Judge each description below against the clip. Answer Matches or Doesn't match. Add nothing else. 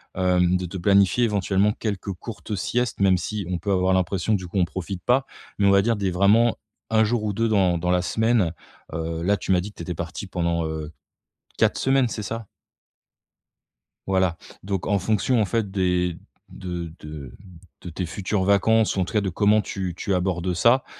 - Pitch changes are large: Doesn't match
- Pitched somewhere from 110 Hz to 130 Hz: Doesn't match